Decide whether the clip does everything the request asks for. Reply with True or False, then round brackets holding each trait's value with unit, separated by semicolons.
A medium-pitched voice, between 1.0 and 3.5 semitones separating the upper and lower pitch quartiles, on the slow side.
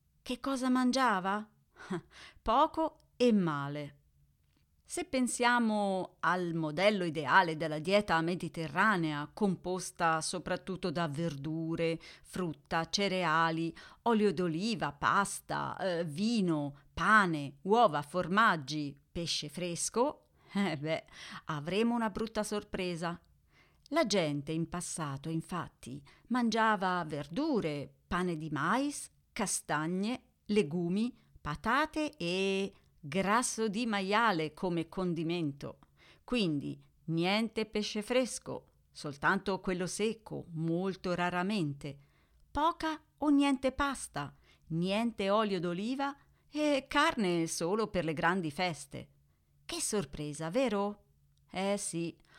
False (180 Hz; 5.2 semitones; 95 wpm)